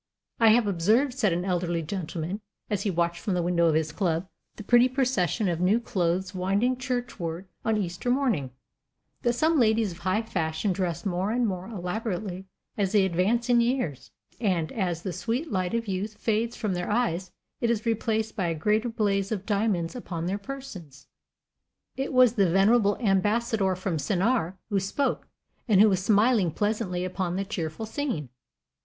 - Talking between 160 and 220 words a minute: Yes, average, 175 wpm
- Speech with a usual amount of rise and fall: Yes, average, 4.3 semitones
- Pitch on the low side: No, high, 200 Hz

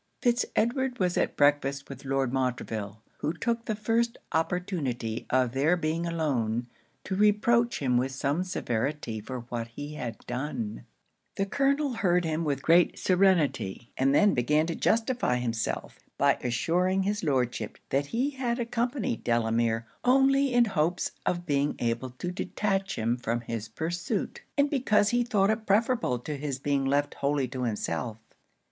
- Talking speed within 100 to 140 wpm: No, average, 155 wpm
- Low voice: No, medium, 150 Hz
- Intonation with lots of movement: Yes, wide, 8.9 semitones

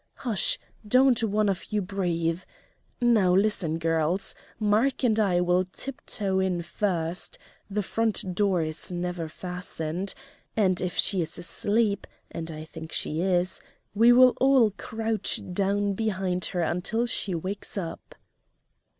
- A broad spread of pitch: No, average, 3.4 semitones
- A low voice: No, high, 190 Hz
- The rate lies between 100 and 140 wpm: Yes, slow, 135 wpm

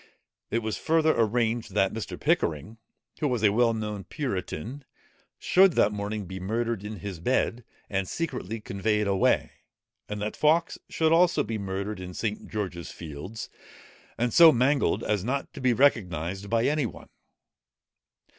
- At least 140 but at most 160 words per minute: Yes, average, 155 wpm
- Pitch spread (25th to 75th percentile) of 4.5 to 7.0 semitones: No, average, 4.1 semitones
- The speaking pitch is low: Yes, low, 110 Hz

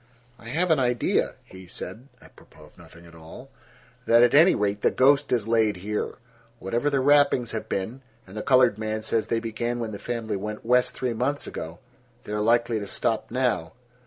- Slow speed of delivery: No, average, 190 wpm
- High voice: No, low, 115 Hz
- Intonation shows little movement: No, average, 3.0 semitones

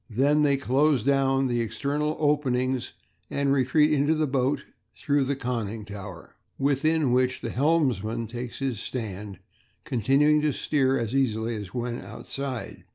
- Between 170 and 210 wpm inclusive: No, average, 140 wpm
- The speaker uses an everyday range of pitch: Yes, average, 3.5 semitones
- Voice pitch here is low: Yes, low, 130 Hz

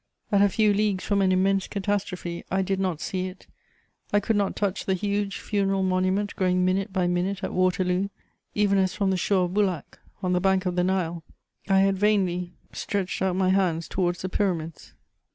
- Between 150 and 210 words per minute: Yes, average, 195 wpm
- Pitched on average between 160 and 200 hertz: Yes, high, 190 Hz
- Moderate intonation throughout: No, narrow, 1.5 semitones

